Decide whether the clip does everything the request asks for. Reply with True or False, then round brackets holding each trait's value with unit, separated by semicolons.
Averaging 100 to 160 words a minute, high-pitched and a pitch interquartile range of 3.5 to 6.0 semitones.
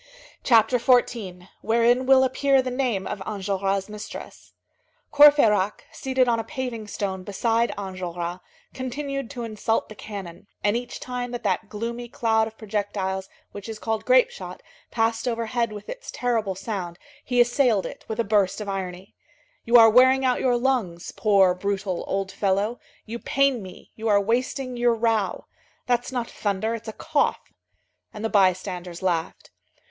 True (155 wpm; 225 Hz; 3.8 semitones)